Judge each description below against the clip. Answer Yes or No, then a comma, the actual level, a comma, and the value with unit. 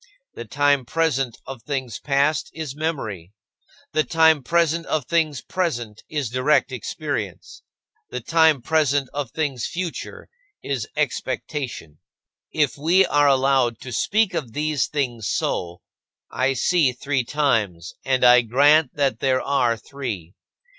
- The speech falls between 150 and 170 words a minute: No, slow, 135 wpm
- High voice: No, medium, 140 Hz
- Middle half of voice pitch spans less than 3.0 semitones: No, average, 3.9 semitones